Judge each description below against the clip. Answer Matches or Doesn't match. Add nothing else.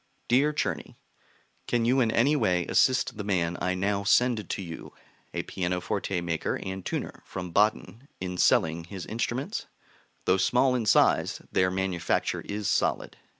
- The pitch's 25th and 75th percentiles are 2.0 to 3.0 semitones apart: Doesn't match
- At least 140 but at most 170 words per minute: Matches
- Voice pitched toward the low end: Matches